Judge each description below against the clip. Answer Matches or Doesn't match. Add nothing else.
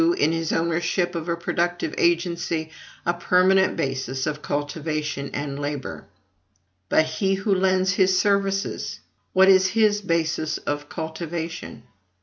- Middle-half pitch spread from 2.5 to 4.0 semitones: Matches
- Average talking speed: Doesn't match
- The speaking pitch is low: Doesn't match